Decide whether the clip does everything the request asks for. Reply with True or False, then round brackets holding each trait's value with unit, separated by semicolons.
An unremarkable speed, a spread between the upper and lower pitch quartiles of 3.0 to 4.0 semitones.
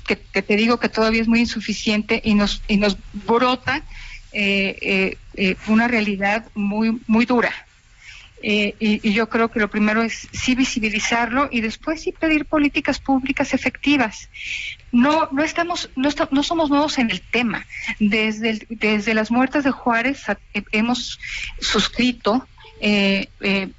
True (160 wpm; 3.7 semitones)